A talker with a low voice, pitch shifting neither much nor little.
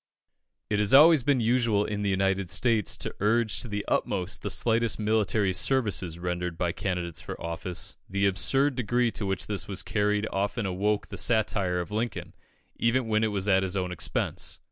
Yes: low, 105 Hz; average, 3.3 semitones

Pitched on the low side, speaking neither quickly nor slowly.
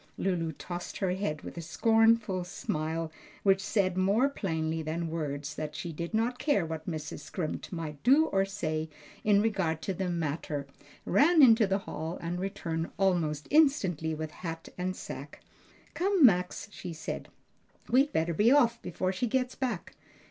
No: medium, 180 Hz; average, 165 wpm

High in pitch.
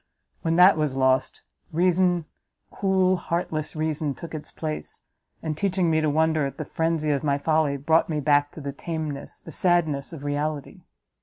No: medium, 155 Hz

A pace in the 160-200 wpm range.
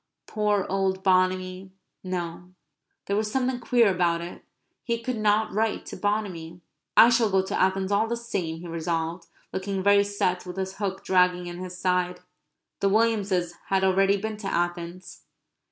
Yes: average, 165 wpm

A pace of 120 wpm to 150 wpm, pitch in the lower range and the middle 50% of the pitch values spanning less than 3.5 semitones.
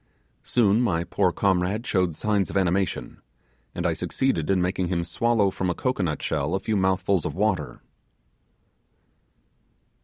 Yes: average, 145 wpm; very low, 95 Hz; average, 2.8 semitones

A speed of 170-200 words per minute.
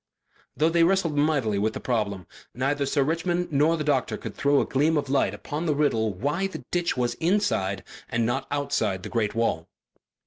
Yes: average, 195 wpm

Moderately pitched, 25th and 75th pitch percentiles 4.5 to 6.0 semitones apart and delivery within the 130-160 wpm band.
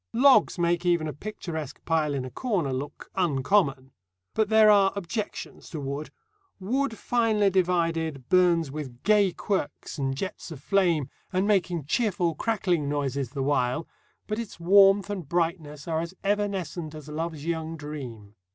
Yes: medium, 170 Hz; average, 5.1 semitones; average, 150 wpm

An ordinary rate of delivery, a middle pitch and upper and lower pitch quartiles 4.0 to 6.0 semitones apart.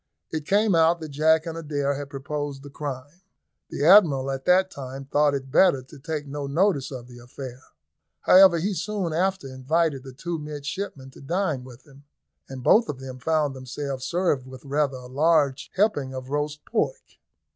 No: average, 180 wpm; medium, 145 Hz; average, 3.6 semitones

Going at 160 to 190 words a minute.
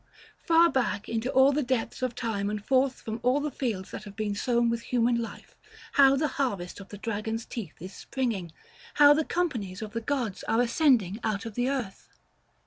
No: average, 200 wpm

